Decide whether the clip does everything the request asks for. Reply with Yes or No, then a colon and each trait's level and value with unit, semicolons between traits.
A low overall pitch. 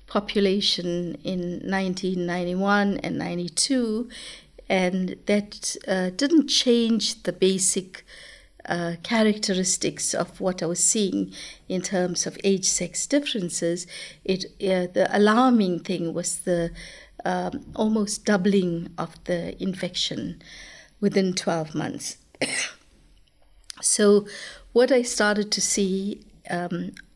No: high, 190 Hz